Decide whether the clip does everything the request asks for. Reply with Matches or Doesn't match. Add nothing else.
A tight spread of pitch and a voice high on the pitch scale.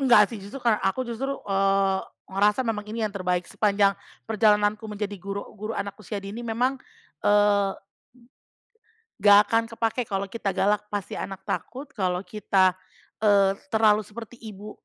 Matches